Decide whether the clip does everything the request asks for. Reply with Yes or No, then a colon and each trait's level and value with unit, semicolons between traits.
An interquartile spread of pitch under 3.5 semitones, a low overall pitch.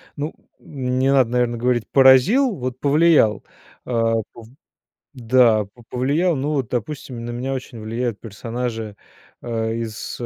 Yes: average, 2.8 semitones; low, 125 Hz